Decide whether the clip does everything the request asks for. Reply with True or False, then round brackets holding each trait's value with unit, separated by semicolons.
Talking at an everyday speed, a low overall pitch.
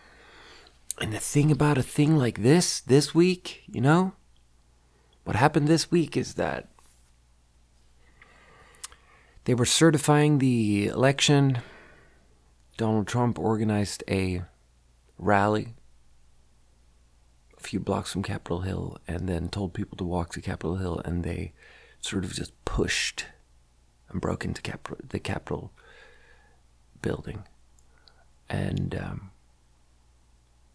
False (115 wpm; 85 Hz)